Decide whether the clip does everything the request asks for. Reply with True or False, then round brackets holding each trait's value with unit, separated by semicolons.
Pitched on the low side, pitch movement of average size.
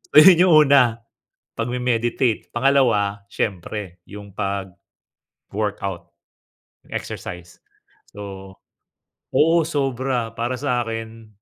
True (115 Hz; 4.0 semitones)